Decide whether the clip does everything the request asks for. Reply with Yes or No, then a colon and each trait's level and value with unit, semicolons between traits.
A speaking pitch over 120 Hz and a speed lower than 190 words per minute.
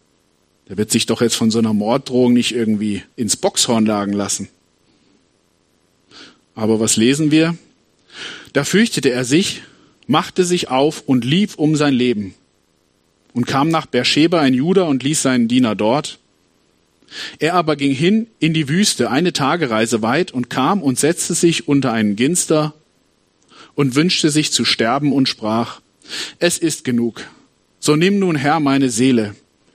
Yes: low, 135 Hz; average, 155 wpm